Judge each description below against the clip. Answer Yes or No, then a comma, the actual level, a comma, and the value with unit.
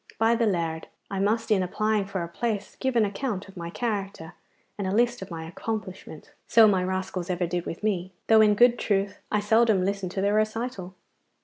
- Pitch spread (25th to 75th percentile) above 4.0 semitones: No, average, 3.0 semitones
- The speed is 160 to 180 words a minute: No, fast, 205 wpm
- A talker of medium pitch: No, high, 200 Hz